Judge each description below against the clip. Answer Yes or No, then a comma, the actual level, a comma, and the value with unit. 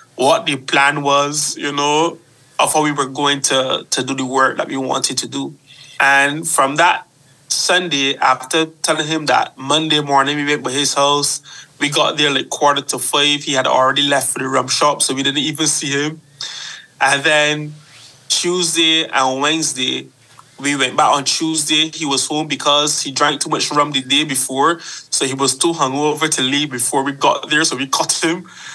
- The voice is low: No, medium, 145 Hz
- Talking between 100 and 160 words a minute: No, average, 195 wpm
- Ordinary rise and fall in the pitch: No, narrow, 2.0 semitones